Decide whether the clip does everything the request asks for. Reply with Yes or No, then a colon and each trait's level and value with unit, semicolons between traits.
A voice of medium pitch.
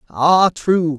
Yes: medium, 160 Hz